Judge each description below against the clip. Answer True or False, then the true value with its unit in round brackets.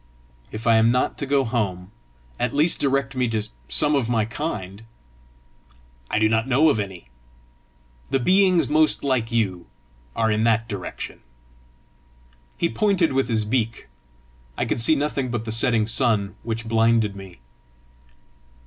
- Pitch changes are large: False (3.8 semitones)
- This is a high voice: False (115 Hz)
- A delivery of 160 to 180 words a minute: False (150 wpm)